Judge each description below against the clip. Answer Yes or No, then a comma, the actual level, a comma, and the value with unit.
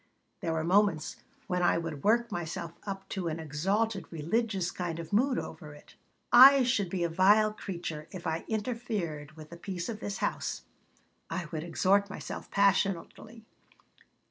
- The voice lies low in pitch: No, medium, 185 Hz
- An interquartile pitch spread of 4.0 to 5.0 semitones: Yes, average, 4.3 semitones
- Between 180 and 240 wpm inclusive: No, average, 160 wpm